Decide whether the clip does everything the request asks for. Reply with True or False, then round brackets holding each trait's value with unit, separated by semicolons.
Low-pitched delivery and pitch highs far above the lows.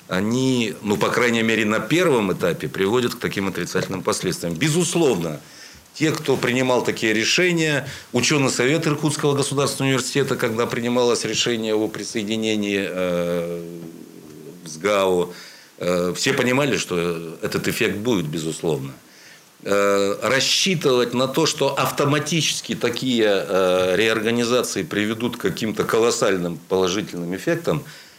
True (115 Hz; 6.3 semitones)